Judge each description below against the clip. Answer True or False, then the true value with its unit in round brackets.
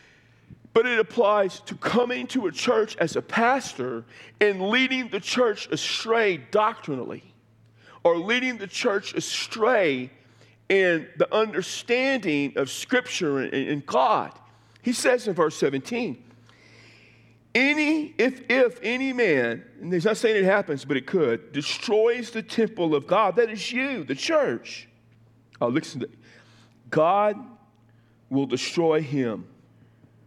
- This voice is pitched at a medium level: True (170 Hz)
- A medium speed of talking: False (130 wpm)